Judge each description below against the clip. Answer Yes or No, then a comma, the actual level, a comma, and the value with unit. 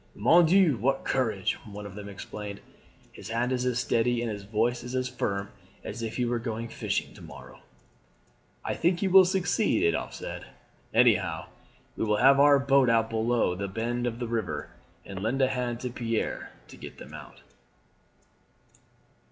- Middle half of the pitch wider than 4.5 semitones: No, average, 3.1 semitones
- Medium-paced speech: Yes, average, 175 wpm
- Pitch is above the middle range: No, low, 120 Hz